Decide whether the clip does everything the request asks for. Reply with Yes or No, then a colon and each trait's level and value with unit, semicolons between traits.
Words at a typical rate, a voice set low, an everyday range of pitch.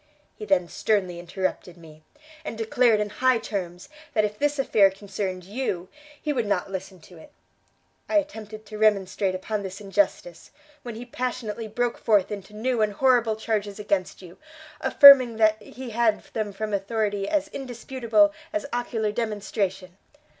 No: average, 155 wpm; high, 215 Hz; average, 3.5 semitones